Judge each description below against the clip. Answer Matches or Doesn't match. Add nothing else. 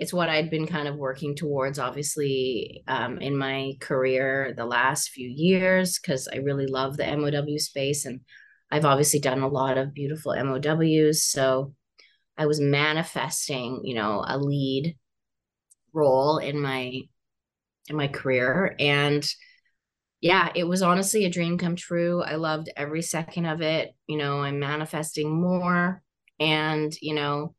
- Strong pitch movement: Doesn't match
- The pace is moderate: Matches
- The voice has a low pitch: Doesn't match